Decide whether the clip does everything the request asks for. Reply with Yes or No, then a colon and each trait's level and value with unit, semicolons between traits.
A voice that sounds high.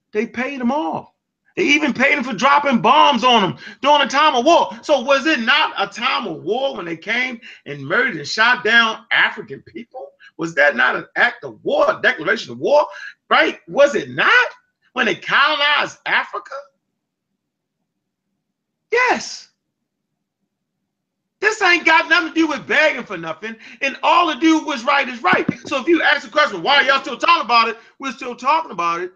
Yes: very high, 280 Hz